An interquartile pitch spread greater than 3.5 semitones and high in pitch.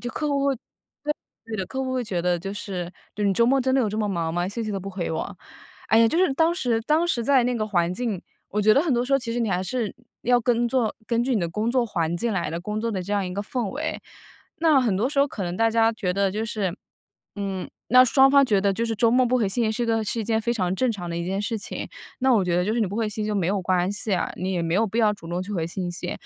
Yes: average, 4.3 semitones; high, 215 Hz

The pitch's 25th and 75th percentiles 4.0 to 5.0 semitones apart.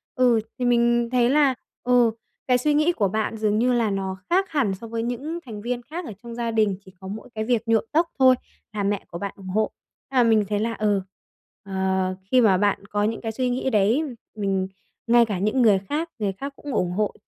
No: average, 3.5 semitones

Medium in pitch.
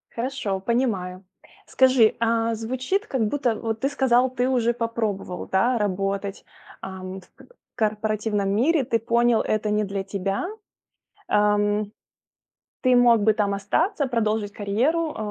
No: high, 220 Hz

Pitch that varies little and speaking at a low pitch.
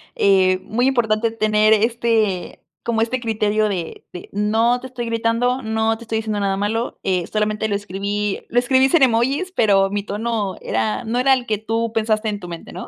No: narrow, 2.3 semitones; high, 220 Hz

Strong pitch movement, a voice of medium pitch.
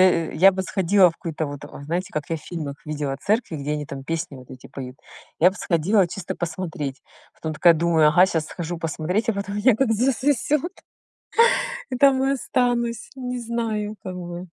Yes: wide, 6.3 semitones; medium, 180 Hz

